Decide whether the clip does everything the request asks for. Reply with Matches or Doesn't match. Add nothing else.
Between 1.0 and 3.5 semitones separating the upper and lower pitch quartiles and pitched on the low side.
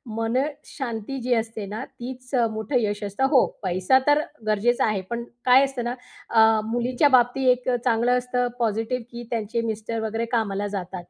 Doesn't match